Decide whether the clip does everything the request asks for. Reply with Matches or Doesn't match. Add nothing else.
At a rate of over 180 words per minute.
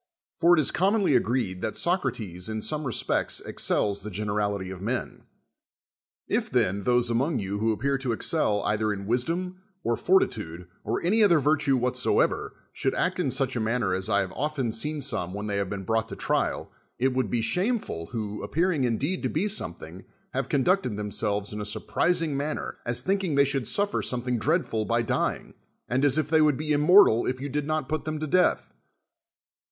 Matches